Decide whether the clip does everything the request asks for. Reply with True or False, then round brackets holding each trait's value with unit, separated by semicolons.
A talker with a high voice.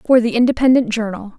True (230 Hz)